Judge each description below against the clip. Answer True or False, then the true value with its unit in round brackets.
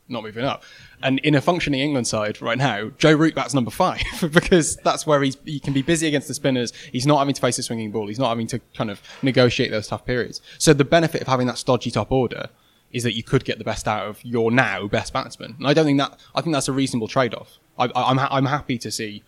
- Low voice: True (130 Hz)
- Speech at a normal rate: False (270 wpm)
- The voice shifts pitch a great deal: False (3.5 semitones)